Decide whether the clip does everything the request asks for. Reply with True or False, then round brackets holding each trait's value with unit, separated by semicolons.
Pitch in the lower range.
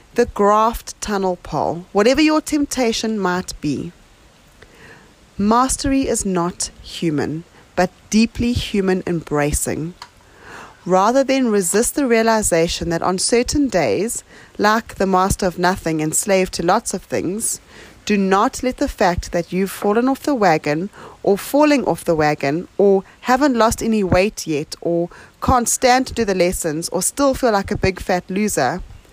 False (195 Hz)